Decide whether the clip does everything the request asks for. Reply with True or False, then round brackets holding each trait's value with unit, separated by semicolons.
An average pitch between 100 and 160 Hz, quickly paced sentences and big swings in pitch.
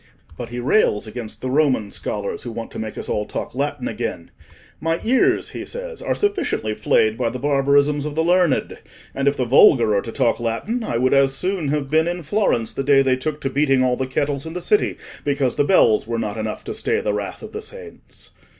True (140 Hz; 225 wpm; 6.4 semitones)